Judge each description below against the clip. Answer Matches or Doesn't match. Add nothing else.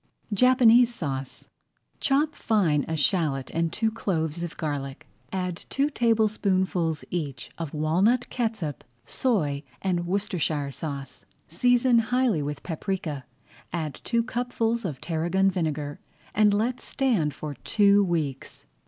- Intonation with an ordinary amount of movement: Doesn't match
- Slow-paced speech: Matches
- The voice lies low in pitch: Doesn't match